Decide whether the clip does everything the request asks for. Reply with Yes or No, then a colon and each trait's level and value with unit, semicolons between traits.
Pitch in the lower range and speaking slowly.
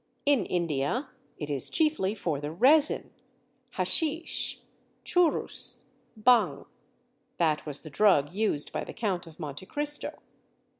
No: medium, 185 Hz; slow, 120 wpm